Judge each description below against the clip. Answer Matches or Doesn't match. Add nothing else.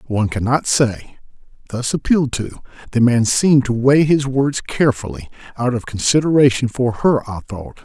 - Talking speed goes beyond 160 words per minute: Matches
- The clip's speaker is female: Doesn't match